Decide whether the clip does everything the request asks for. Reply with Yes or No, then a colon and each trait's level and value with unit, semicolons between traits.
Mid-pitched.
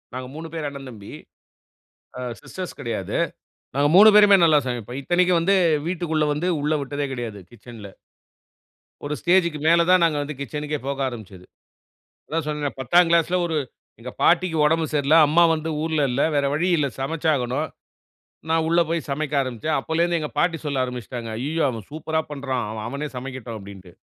Yes: medium, 150 Hz